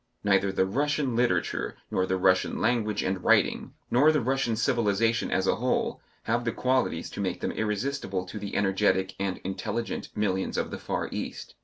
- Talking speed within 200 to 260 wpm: No, average, 175 wpm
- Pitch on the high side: No, low, 105 Hz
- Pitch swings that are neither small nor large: Yes, average, 4.2 semitones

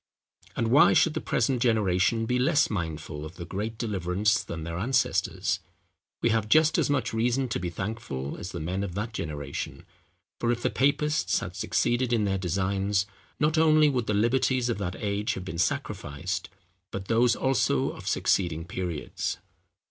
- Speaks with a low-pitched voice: Yes, low, 105 Hz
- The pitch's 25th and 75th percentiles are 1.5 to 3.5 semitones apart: No, average, 5.3 semitones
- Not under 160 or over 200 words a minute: Yes, average, 170 wpm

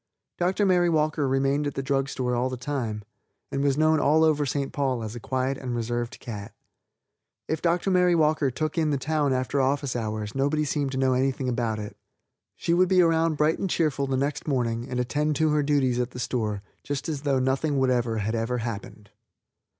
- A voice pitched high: No, low, 135 Hz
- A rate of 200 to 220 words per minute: Yes, fast, 205 wpm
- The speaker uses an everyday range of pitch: Yes, average, 3.6 semitones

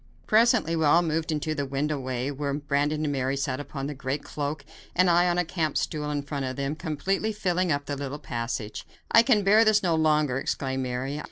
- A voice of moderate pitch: Yes, medium, 150 Hz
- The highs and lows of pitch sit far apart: No, average, 3.5 semitones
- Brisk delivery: Yes, fast, 215 wpm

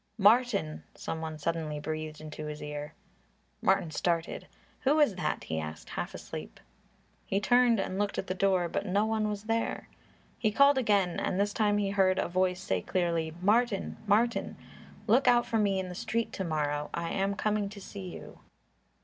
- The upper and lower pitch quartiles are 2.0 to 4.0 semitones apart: No, average, 4.6 semitones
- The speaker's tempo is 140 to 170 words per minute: No, average, 185 wpm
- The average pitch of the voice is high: Yes, high, 195 Hz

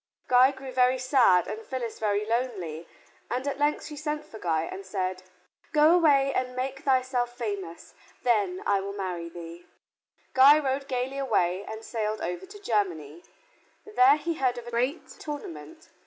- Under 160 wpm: No, average, 165 wpm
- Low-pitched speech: No, high, 245 Hz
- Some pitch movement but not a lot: No, wide, 6.1 semitones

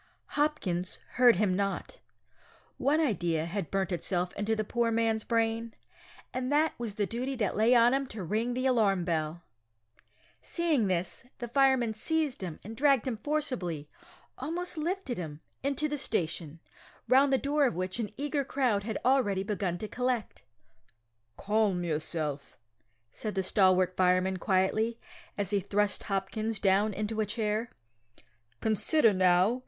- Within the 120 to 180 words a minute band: Yes, average, 150 wpm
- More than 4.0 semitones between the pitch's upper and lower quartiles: Yes, average, 5.3 semitones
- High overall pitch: Yes, high, 215 Hz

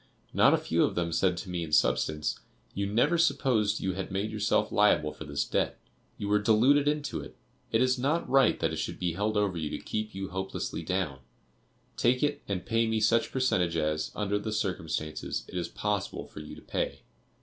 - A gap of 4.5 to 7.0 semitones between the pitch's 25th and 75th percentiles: Yes, average, 4.8 semitones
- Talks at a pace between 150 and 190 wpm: No, fast, 205 wpm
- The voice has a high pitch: No, low, 100 Hz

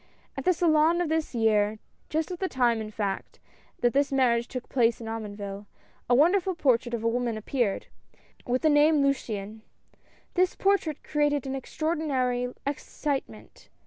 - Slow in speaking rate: No, average, 165 wpm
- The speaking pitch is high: Yes, very high, 260 Hz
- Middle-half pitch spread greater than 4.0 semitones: Yes, average, 5.2 semitones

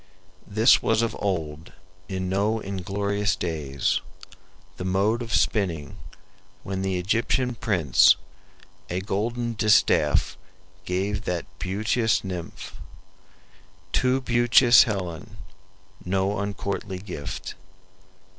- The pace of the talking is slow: Yes, slow, 95 wpm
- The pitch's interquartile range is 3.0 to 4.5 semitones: Yes, average, 3.4 semitones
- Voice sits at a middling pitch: No, low, 100 Hz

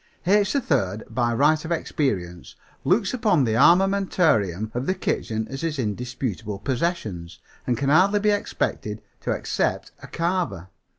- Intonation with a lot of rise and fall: Yes, wide, 8.9 semitones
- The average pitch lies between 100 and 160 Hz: Yes, low, 135 Hz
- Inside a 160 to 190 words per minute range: No, average, 140 wpm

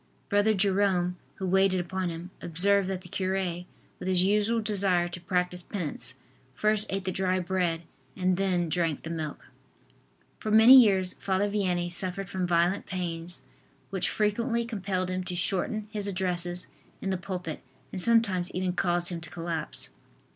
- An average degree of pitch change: No, narrow, 2.1 semitones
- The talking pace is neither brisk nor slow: Yes, average, 160 wpm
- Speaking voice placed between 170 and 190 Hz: Yes, medium, 185 Hz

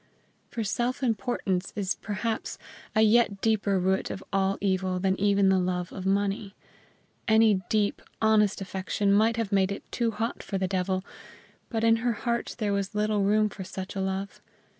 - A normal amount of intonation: No, narrow, 2.3 semitones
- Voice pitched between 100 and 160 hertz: No, high, 200 Hz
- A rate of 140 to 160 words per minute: No, average, 175 wpm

